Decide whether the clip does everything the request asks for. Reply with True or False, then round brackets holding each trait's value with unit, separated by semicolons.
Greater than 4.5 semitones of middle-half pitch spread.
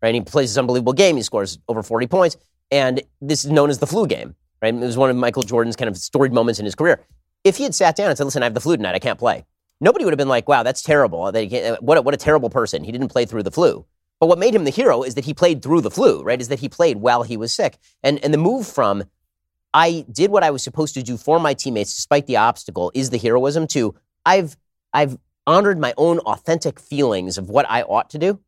True (5.1 semitones)